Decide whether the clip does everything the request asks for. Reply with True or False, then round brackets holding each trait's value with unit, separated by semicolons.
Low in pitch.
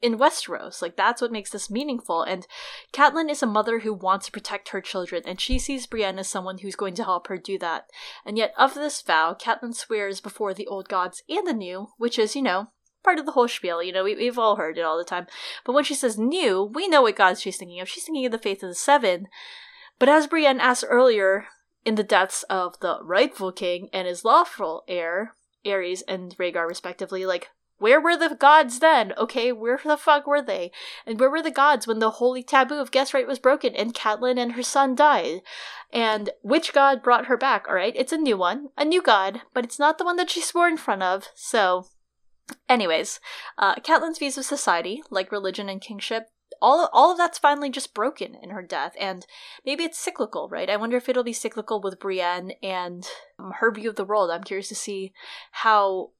False (230 Hz)